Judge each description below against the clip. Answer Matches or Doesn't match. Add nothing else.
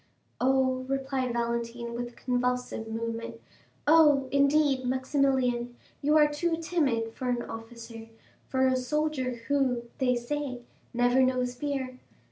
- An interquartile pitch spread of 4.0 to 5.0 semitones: Doesn't match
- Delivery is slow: Matches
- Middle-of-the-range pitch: Doesn't match